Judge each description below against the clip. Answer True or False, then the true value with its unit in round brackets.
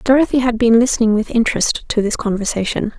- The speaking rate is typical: True (180 wpm)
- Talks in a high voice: True (230 Hz)